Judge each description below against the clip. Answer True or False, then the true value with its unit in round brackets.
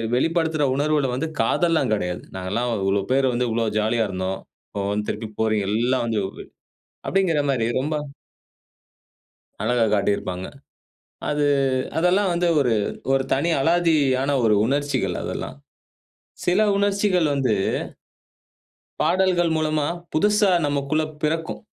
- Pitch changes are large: True (6.5 semitones)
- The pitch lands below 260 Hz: True (140 Hz)